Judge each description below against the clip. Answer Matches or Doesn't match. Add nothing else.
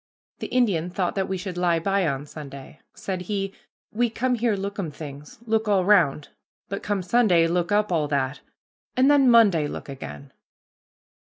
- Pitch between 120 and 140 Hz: Doesn't match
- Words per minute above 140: Matches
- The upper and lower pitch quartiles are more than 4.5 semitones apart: Matches